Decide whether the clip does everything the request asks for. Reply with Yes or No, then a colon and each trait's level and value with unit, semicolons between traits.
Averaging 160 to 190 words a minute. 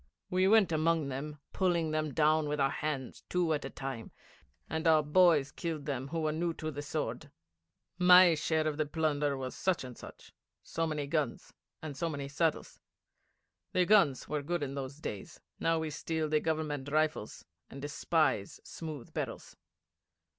Yes: average, 170 wpm